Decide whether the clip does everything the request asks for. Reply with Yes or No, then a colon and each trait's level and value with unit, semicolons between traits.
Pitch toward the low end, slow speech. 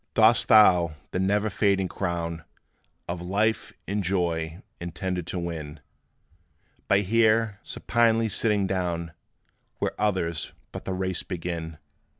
Yes: very low, 95 Hz; slow, 120 wpm